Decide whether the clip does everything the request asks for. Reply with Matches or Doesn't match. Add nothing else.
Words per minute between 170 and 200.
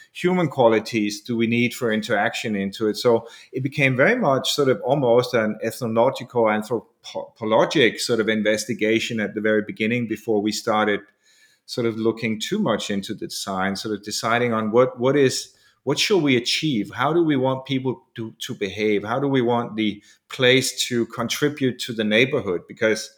Matches